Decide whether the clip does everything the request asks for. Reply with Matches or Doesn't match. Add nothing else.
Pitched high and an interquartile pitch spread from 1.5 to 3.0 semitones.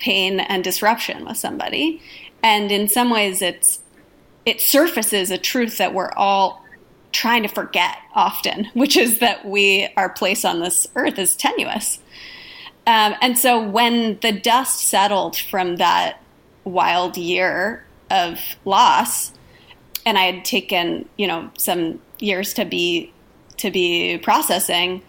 Doesn't match